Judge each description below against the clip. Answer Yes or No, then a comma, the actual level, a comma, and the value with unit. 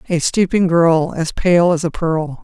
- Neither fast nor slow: Yes, average, 195 wpm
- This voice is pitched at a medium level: Yes, medium, 170 Hz